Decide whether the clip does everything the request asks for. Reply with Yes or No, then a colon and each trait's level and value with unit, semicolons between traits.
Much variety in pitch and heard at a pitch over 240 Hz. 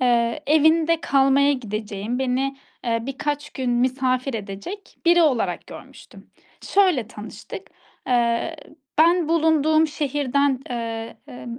No: average, 4.6 semitones; very high, 265 Hz